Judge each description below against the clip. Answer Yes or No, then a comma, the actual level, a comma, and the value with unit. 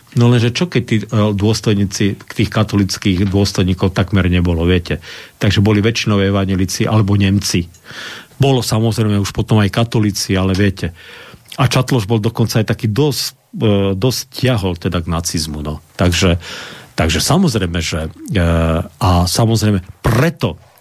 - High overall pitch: No, low, 105 Hz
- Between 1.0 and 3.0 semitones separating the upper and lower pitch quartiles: No, average, 3.7 semitones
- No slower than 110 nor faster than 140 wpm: Yes, average, 135 wpm